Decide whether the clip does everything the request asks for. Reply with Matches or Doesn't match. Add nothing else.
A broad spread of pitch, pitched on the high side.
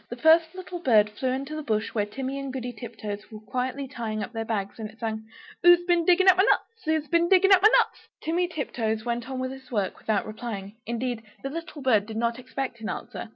Matches